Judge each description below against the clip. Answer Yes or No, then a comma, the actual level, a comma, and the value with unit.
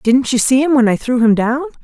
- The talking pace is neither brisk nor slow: No, fast, 295 wpm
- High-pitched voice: Yes, very high, 255 Hz